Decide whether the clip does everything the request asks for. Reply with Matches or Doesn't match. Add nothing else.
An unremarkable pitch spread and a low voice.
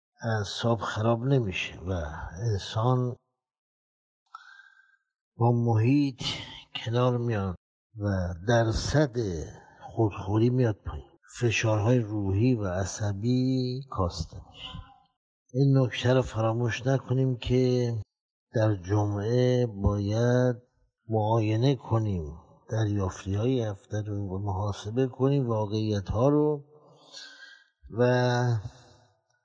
Matches